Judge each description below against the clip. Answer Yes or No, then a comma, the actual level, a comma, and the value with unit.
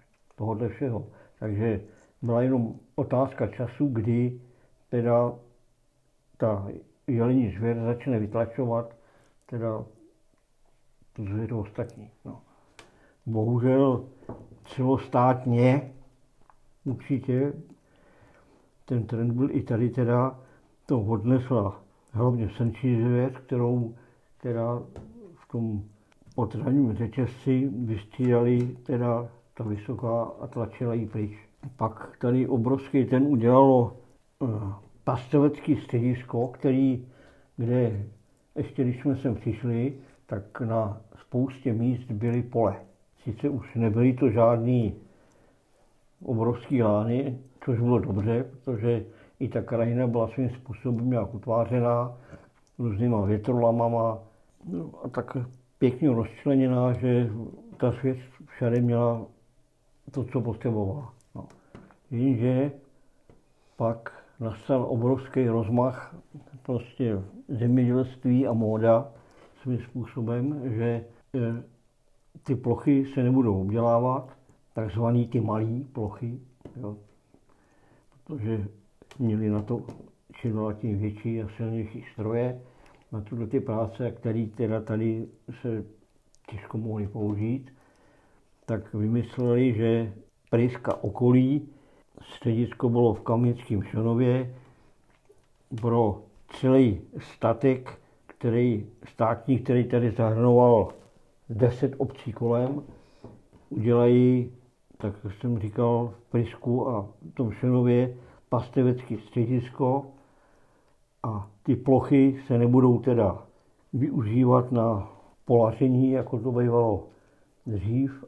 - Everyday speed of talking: No, slow, 95 wpm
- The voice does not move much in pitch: Yes, narrow, 2.2 semitones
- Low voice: Yes, low, 120 Hz